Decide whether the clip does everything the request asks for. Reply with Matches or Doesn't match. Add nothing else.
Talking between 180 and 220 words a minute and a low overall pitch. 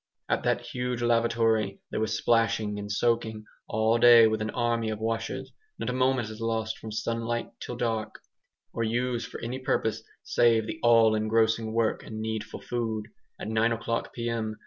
Doesn't match